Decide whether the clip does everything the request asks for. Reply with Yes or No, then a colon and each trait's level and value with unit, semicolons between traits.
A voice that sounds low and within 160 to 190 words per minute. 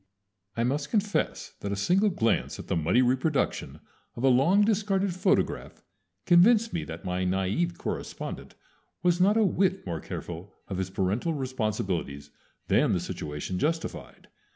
No: low, 130 Hz; average, 150 wpm